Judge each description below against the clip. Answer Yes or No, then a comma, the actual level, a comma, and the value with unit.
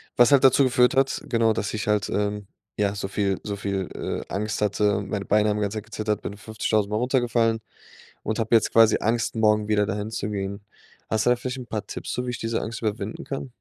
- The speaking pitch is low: Yes, low, 110 Hz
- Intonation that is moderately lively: No, narrow, 2.0 semitones